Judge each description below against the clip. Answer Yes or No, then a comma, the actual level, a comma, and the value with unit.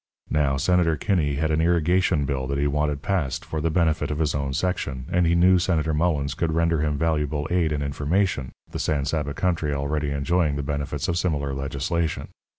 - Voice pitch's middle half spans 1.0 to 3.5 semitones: Yes, average, 3.0 semitones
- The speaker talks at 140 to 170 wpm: No, average, 195 wpm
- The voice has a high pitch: No, very low, 75 Hz